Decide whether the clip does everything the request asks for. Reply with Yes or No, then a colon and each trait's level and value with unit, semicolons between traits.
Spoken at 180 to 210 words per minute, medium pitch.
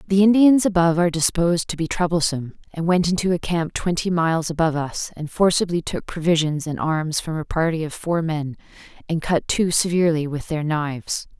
Yes: average, 190 wpm; medium, 165 Hz